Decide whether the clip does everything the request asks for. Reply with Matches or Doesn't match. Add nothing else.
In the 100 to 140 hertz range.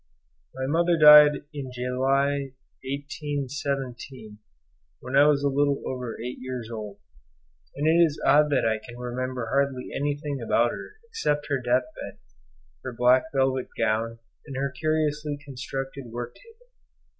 Matches